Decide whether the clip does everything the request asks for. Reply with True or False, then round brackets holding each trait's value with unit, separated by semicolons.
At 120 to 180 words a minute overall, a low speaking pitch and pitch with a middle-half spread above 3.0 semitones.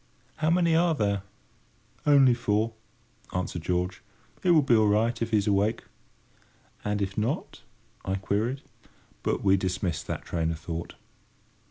True (145 wpm; 105 Hz; 4.9 semitones)